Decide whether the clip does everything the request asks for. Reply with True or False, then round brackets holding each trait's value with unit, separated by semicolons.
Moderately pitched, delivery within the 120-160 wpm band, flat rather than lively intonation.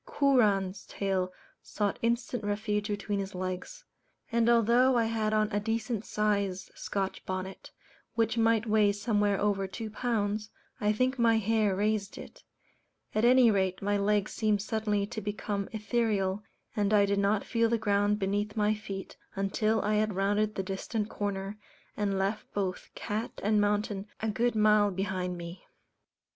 False (210 Hz; 155 wpm; 1.8 semitones)